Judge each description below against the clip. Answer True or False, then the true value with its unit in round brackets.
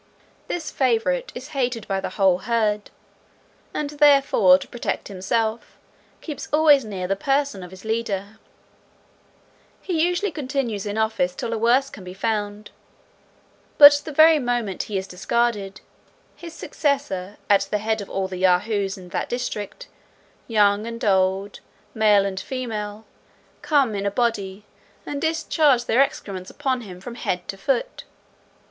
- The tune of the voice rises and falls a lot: True (5.7 semitones)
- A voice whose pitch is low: False (220 Hz)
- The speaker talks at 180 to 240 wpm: False (150 wpm)